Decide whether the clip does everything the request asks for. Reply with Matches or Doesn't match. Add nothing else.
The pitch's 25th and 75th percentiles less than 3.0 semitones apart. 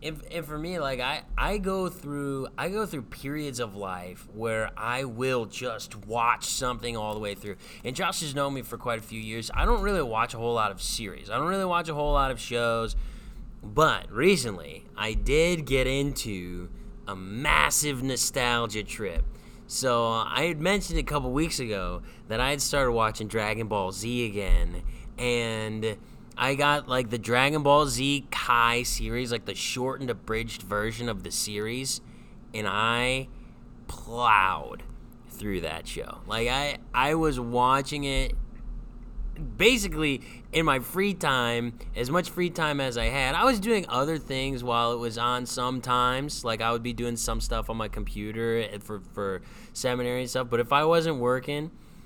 Doesn't match